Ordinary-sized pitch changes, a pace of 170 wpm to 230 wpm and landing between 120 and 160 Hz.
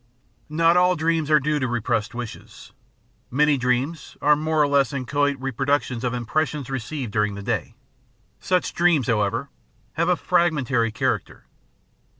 No: average, 4.2 semitones; average, 150 wpm; medium, 140 Hz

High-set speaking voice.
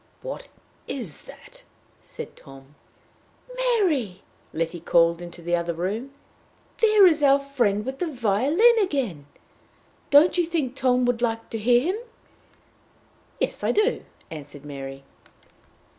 Yes: high, 245 Hz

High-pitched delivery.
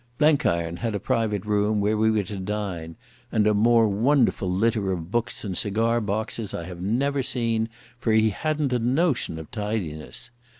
No: low, 110 Hz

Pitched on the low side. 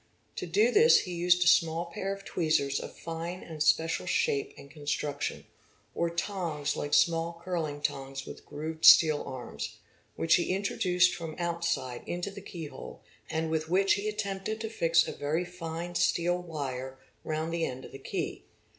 No: medium, 170 Hz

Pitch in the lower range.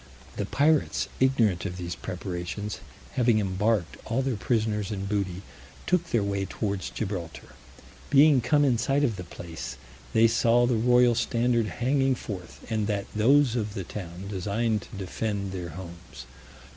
Yes: low, 105 Hz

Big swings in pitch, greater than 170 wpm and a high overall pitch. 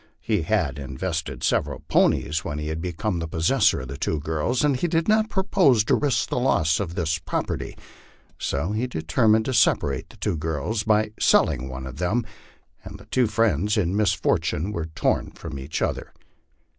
No: wide, 6.3 semitones; average, 180 wpm; very low, 90 Hz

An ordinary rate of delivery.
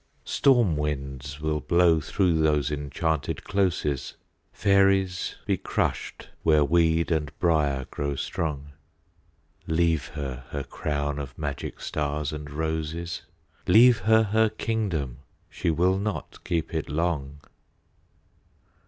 No: slow, 110 wpm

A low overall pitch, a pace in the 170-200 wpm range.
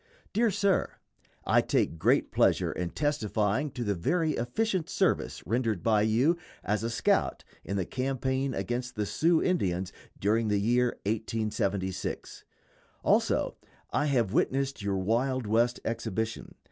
No: low, 115 Hz; average, 145 wpm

